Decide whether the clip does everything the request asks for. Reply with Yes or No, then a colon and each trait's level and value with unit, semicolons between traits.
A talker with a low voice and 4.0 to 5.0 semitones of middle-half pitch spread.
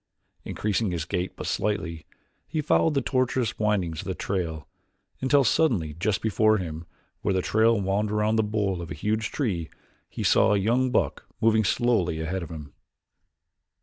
Yes: low, 105 Hz; average, 4.3 semitones